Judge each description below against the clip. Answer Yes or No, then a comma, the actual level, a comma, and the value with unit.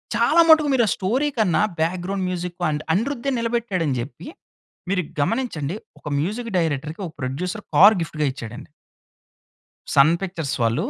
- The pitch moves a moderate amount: No, wide, 6.9 semitones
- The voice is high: No, medium, 180 Hz